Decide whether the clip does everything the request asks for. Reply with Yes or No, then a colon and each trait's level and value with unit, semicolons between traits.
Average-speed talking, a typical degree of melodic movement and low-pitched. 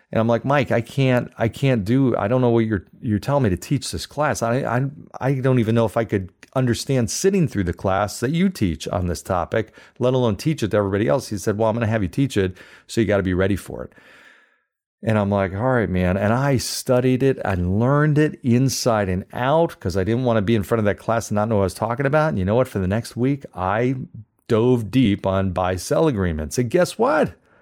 No: fast, 255 wpm; average, 4.5 semitones; low, 115 Hz